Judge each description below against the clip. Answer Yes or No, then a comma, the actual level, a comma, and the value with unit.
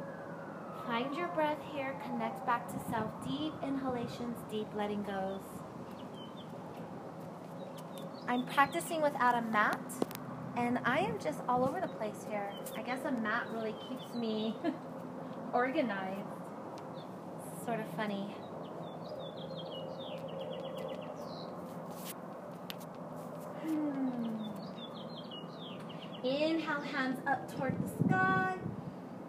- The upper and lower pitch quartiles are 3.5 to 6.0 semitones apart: Yes, average, 4.1 semitones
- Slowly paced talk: Yes, slow, 95 wpm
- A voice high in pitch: Yes, high, 235 Hz